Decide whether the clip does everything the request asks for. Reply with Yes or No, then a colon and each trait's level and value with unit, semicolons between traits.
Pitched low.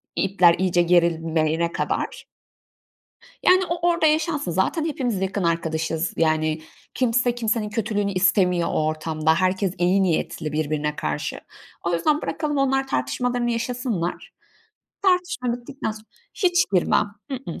No: high, 195 Hz